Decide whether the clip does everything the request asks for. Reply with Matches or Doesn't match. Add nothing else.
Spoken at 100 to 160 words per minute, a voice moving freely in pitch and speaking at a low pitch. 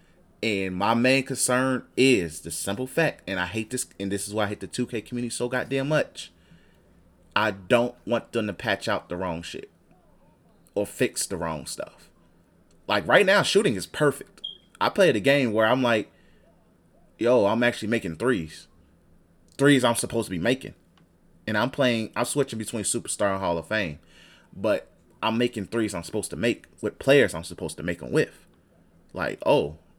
Doesn't match